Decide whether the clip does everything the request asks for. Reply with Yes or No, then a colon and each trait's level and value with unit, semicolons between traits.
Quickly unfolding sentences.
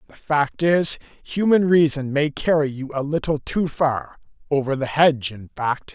No: average, 160 wpm